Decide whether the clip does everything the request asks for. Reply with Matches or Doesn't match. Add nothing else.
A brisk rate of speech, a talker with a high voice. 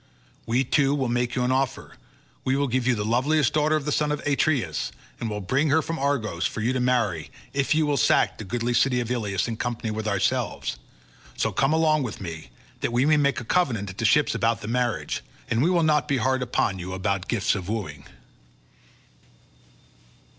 Doesn't match